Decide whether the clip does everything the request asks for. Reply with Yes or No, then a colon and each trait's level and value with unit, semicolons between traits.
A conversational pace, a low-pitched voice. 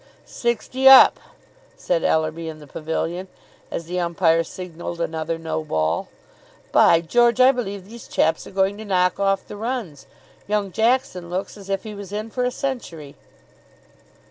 No: average, 160 wpm; high, 190 Hz